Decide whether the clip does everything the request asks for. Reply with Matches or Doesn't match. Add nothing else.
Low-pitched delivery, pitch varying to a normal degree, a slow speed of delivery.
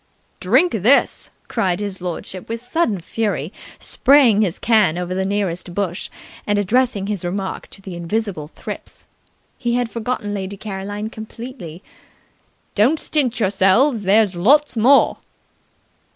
Doesn't match